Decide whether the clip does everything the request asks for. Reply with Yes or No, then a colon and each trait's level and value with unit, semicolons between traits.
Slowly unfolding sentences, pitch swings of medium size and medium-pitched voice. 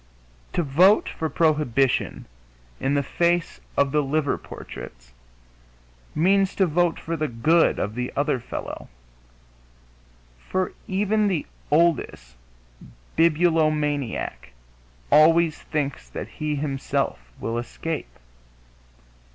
Yes: slow, 100 wpm; average, 4.0 semitones; medium, 150 Hz